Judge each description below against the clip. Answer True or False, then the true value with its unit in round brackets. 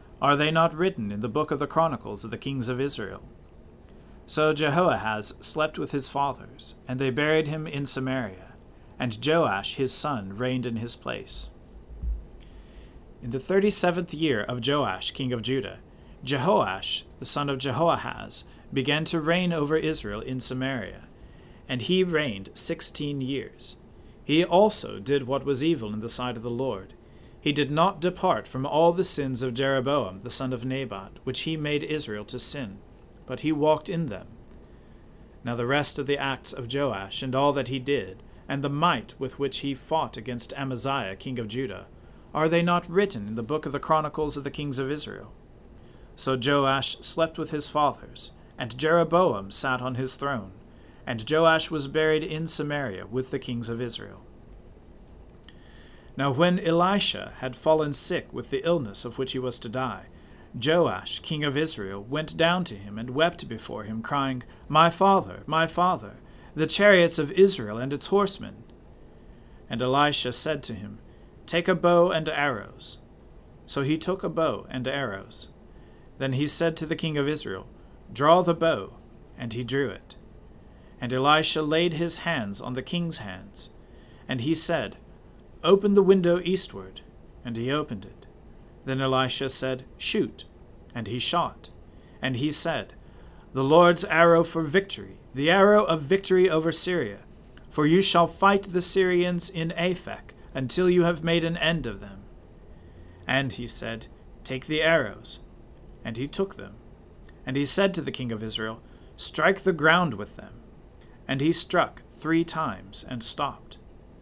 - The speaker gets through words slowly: False (170 wpm)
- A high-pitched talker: False (140 Hz)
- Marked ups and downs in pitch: False (5.0 semitones)